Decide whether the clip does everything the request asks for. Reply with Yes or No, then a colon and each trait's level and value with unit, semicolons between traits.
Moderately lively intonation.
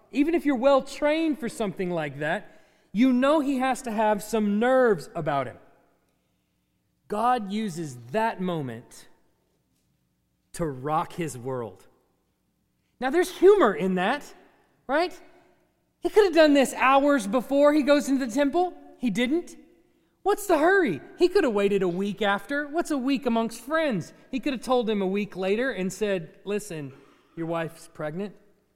No: wide, 7.4 semitones